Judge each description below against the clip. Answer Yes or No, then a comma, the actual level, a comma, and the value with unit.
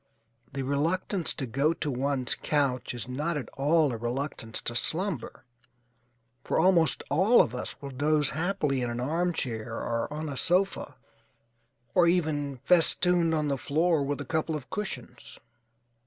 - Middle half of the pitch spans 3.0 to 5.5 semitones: Yes, average, 4.1 semitones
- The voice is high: No, medium, 145 Hz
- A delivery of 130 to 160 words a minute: Yes, average, 155 wpm